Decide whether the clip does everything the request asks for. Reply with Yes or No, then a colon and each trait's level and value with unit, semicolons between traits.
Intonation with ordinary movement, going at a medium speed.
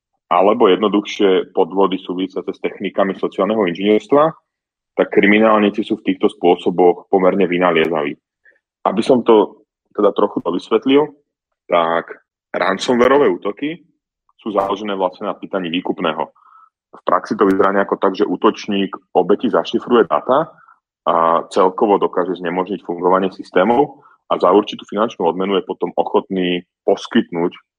Yes: average, 3.1 semitones; average, 125 wpm